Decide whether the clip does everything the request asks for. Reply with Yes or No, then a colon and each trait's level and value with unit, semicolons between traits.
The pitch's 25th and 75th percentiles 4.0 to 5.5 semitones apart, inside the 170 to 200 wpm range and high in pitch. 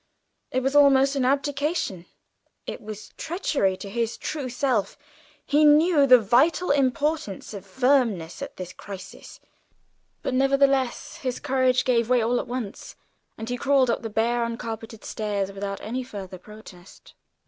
No: average, 4.5 semitones; average, 150 wpm; high, 245 Hz